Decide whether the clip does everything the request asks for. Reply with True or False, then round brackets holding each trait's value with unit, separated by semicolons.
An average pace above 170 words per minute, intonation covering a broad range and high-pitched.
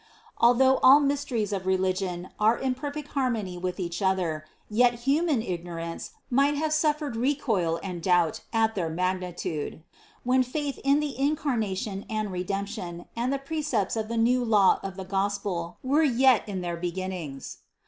False (160 wpm; 6.4 semitones; 215 Hz)